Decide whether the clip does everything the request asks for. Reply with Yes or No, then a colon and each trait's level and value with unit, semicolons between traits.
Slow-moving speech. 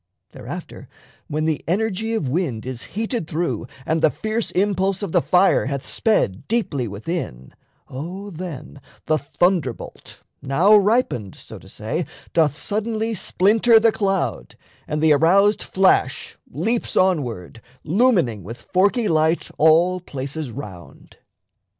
Yes: slow, 130 wpm